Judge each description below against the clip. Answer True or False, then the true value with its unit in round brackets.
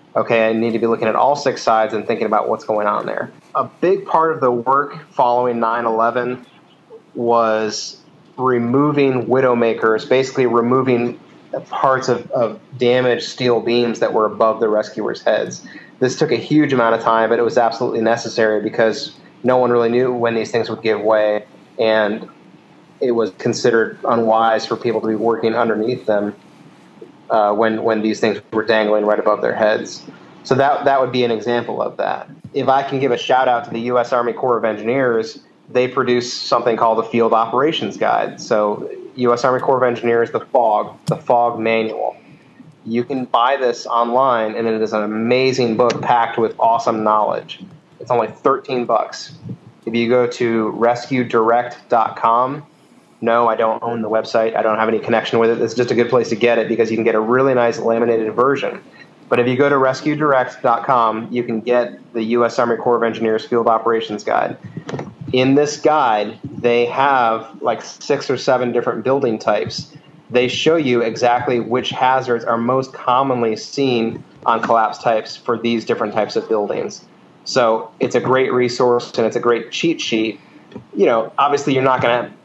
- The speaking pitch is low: True (120 Hz)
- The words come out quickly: False (185 wpm)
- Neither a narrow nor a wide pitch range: False (2.0 semitones)